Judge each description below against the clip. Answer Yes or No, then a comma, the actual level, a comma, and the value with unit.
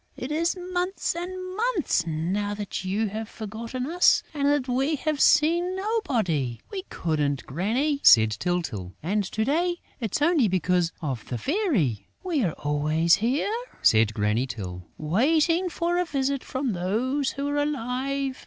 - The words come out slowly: No, average, 155 wpm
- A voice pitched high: Yes, very high, 250 Hz